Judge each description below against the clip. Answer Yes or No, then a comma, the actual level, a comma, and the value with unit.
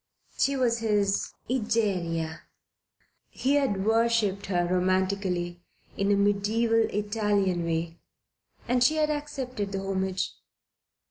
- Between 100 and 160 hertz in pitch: No, high, 200 Hz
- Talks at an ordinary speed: No, slow, 110 wpm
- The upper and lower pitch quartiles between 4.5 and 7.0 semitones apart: No, average, 3.6 semitones